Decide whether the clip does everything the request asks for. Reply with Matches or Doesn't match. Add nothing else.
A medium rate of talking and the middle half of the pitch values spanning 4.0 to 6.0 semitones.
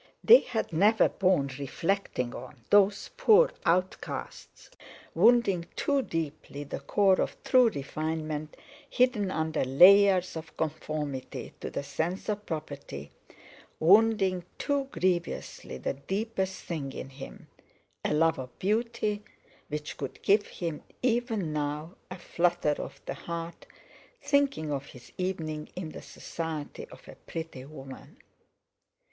Doesn't match